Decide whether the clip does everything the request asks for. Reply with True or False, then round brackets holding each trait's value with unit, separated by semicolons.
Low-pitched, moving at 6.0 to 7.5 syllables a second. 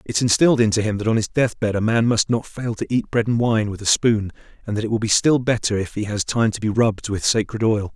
True (110 Hz; 6.1 syllables/s)